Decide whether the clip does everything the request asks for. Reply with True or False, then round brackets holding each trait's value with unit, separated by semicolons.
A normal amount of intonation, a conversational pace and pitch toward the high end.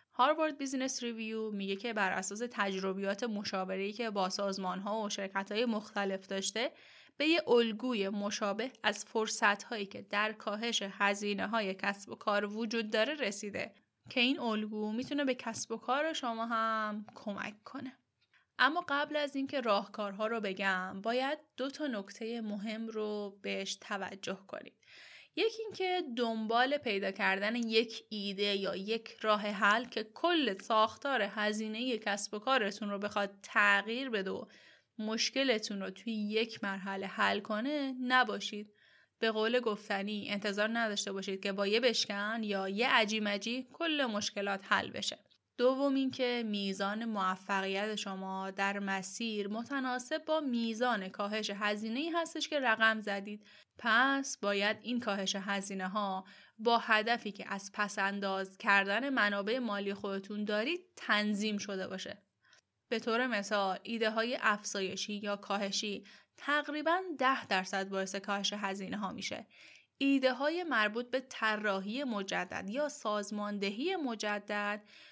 True (3.3 semitones; 140 wpm; 215 Hz)